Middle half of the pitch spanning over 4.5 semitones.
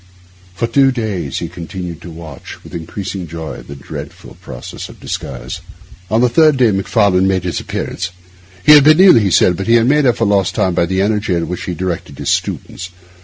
Yes: average, 5.0 semitones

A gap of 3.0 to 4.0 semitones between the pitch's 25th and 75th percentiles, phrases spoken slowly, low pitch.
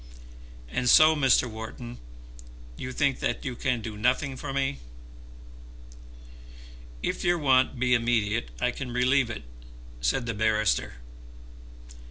Yes: average, 3.3 semitones; slow, 125 wpm; low, 125 Hz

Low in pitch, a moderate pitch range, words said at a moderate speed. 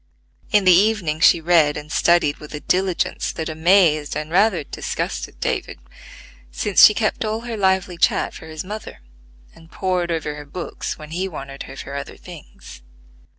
No: medium, 170 Hz; average, 3.9 semitones; average, 170 wpm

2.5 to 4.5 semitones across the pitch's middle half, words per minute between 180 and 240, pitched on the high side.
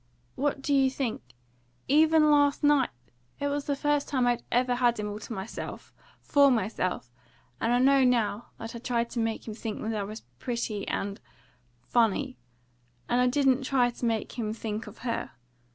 Yes: average, 3.5 semitones; average, 185 wpm; high, 245 Hz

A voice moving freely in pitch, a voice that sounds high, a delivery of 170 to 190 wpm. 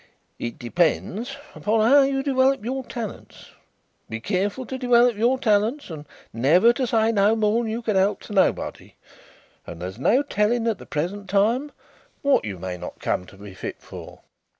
Yes: wide, 5.7 semitones; high, 215 Hz; average, 175 wpm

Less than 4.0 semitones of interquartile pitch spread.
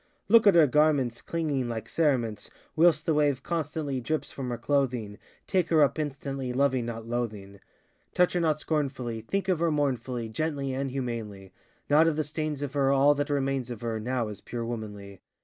No: average, 4.5 semitones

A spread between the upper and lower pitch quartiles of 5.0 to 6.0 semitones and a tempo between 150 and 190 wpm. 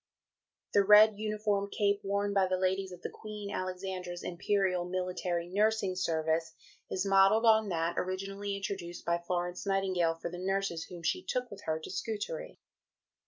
No: narrow, 2.4 semitones; average, 160 wpm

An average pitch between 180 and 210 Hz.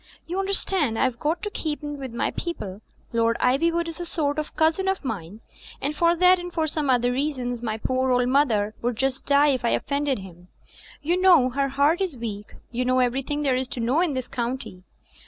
No: very high, 270 Hz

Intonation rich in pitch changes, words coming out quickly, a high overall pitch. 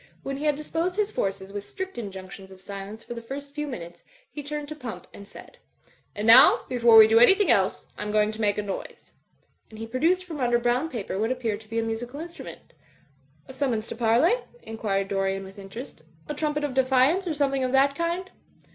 Yes: wide, 5.8 semitones; fast, 215 wpm; high, 240 Hz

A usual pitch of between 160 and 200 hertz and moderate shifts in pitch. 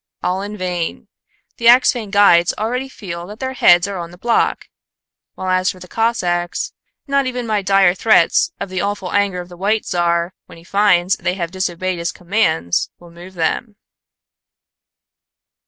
Yes: medium, 185 Hz; average, 3.3 semitones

